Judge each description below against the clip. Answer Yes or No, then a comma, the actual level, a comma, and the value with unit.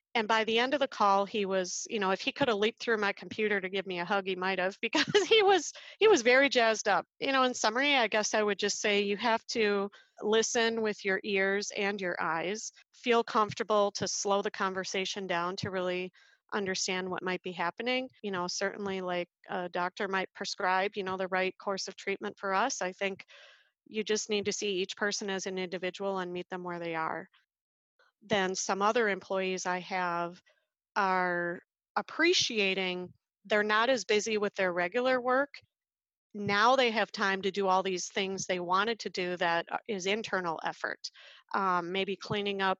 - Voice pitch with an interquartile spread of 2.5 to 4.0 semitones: Yes, average, 3.2 semitones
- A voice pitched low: No, high, 200 Hz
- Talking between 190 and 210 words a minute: Yes, average, 200 wpm